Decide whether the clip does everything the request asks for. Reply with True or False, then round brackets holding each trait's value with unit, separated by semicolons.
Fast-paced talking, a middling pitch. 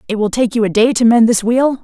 False (325 wpm; 230 Hz)